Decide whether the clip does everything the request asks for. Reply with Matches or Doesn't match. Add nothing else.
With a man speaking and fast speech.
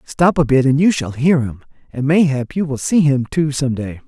Matches